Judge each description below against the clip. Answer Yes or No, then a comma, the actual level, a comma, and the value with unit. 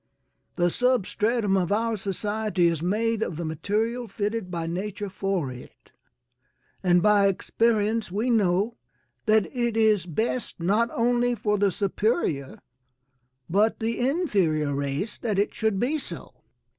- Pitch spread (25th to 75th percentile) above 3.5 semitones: Yes, average, 4.0 semitones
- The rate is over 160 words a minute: No, slow, 135 wpm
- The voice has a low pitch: No, high, 210 Hz